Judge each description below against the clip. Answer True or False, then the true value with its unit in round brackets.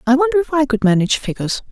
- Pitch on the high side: True (260 Hz)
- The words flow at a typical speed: False (245 wpm)